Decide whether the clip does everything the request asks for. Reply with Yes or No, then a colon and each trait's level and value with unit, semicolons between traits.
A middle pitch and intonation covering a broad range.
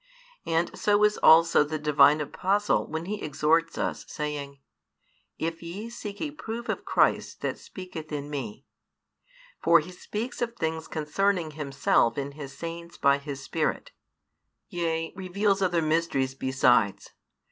No: medium, 160 Hz; average, 4.2 semitones